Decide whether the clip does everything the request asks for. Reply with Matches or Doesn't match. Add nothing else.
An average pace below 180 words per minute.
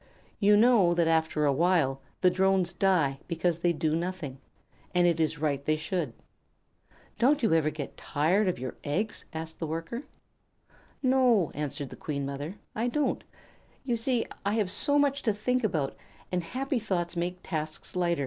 Matches